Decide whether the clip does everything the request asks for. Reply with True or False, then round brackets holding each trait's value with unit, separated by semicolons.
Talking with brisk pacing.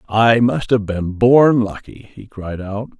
False (180 wpm)